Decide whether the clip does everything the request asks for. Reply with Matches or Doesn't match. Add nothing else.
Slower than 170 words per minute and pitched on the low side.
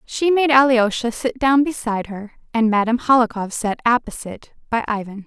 Doesn't match